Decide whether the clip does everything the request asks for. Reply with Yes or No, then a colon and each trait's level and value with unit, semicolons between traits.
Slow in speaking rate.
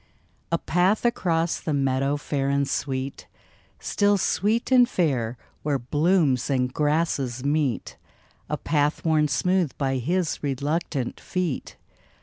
Yes: slow, 125 wpm